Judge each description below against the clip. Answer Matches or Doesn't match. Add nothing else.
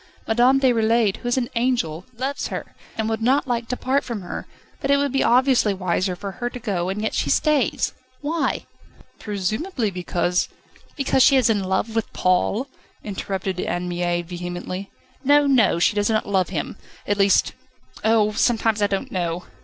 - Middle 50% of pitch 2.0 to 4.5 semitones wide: Doesn't match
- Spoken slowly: Doesn't match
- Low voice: Doesn't match